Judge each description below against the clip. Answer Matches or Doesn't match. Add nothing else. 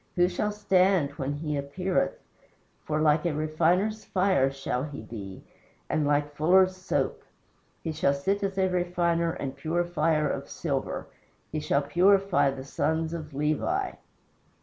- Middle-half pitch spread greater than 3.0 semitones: Matches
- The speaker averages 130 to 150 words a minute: Matches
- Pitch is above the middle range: Doesn't match